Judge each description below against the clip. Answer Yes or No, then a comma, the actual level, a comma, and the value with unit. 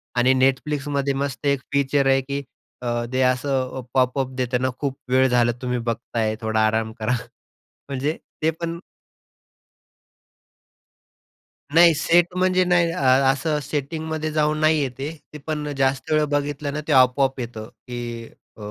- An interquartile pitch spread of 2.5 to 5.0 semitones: Yes, average, 3.0 semitones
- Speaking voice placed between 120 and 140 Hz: Yes, low, 135 Hz